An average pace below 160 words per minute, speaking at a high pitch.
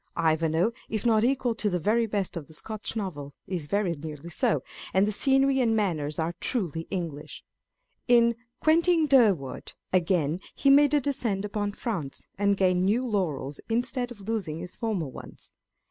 No: average, 165 wpm; high, 200 Hz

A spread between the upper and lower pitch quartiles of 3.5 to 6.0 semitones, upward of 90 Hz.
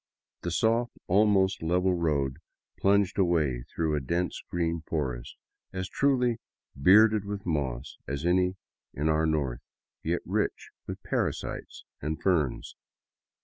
No: average, 4.5 semitones; very low, 85 Hz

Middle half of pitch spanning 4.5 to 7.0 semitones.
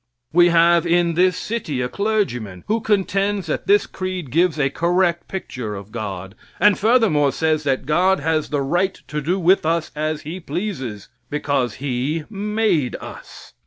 Yes: average, 5.2 semitones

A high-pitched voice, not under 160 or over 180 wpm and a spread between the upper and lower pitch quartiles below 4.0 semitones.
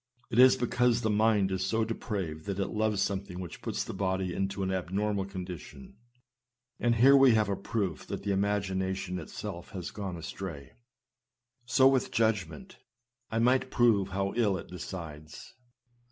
No: low, 100 Hz; average, 170 wpm; average, 3.1 semitones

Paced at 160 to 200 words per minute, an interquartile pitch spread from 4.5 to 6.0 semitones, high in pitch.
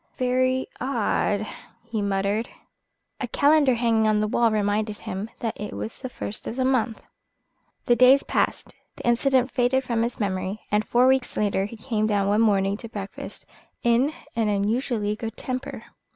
No: average, 165 wpm; average, 3.3 semitones; high, 225 Hz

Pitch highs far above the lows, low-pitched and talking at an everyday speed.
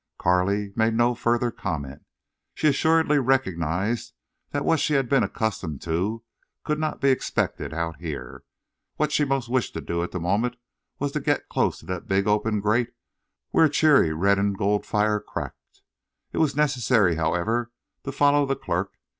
Yes: wide, 6.8 semitones; low, 110 Hz; average, 170 wpm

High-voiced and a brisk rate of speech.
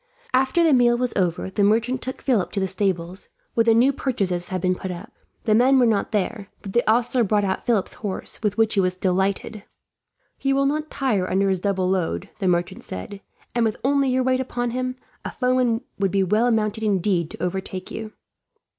Yes: high, 215 Hz; fast, 210 wpm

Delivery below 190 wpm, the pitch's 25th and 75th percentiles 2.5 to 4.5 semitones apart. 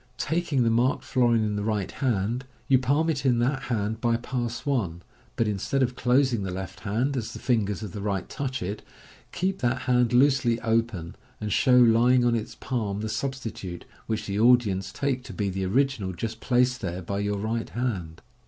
No: average, 195 wpm; average, 3.9 semitones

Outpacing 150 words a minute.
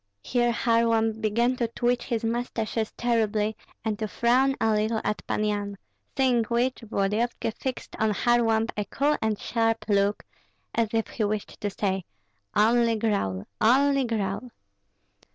No: average, 145 wpm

